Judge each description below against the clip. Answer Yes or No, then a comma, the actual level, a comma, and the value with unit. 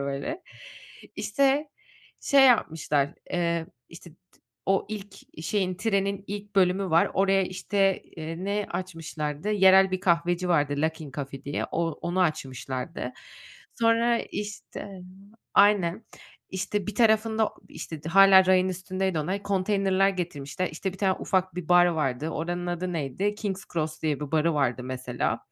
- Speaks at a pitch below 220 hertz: Yes, medium, 185 Hz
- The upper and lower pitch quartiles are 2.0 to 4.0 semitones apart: Yes, average, 3.7 semitones